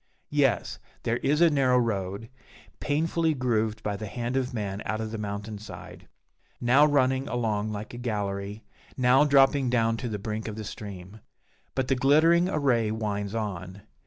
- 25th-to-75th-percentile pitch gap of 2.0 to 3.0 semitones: No, average, 4.3 semitones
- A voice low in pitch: Yes, low, 115 Hz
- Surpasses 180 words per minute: No, average, 165 wpm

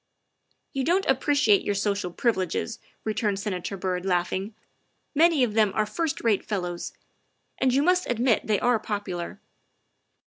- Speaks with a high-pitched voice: Yes, high, 215 Hz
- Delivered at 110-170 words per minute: Yes, average, 165 wpm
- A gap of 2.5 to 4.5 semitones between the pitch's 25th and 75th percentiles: No, average, 4.9 semitones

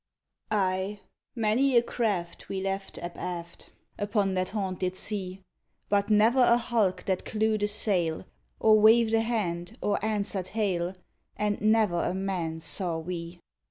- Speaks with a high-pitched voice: Yes, high, 200 Hz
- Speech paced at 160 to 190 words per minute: No, average, 140 wpm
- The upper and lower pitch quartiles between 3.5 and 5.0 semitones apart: No, average, 3.0 semitones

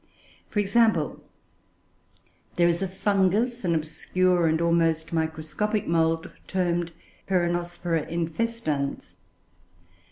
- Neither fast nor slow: No, slow, 90 wpm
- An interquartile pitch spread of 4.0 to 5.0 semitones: No, average, 3.0 semitones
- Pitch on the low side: No, medium, 175 Hz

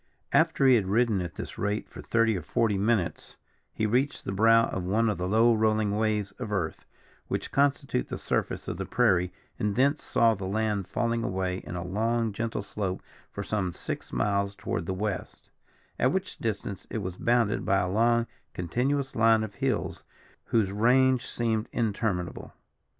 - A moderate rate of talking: Yes, average, 175 wpm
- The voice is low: Yes, low, 110 Hz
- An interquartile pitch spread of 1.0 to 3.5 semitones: Yes, average, 3.1 semitones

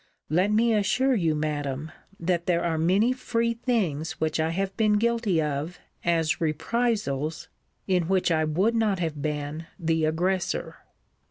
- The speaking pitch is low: No, medium, 170 Hz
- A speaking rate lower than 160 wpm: Yes, average, 150 wpm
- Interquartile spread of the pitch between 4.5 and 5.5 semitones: Yes, average, 5.0 semitones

